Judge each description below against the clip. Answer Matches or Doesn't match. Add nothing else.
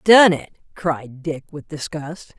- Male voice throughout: Doesn't match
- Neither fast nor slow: Matches